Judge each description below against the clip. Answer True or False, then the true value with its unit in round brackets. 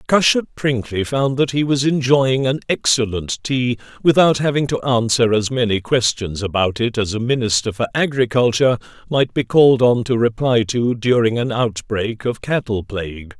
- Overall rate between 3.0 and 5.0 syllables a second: True (4.9 syllables/s)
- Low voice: True (120 Hz)